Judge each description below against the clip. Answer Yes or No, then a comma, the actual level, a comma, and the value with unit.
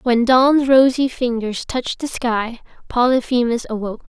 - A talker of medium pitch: No, high, 245 Hz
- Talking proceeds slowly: Yes, slow, 130 wpm